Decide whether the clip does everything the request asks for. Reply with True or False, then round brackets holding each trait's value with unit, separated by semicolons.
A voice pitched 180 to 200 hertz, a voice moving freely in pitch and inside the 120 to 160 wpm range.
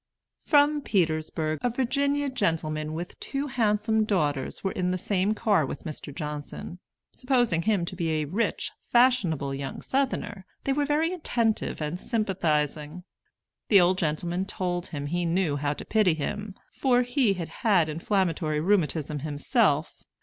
True (185 Hz; 6.6 semitones; 150 wpm)